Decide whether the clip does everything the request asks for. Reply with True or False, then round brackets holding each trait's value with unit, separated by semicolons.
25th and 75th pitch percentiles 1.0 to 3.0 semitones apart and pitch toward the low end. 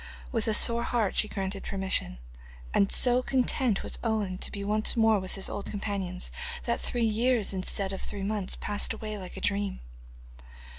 False (2.5 semitones; 205 Hz)